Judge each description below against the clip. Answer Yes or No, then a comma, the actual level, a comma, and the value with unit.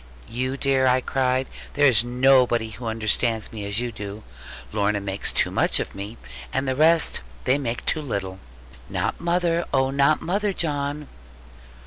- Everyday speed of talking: Yes, average, 160 wpm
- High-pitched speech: No, low, 130 Hz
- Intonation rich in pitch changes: No, average, 4.3 semitones